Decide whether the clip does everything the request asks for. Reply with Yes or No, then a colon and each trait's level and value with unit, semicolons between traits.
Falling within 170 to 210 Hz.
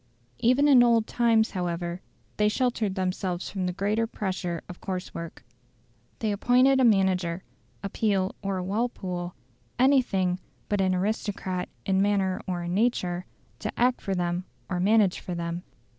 Yes: high, 190 Hz